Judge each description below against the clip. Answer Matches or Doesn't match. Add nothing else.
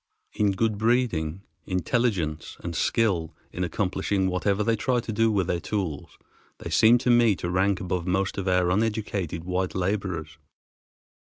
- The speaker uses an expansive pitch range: Doesn't match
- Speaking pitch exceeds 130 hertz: Doesn't match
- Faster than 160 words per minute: Doesn't match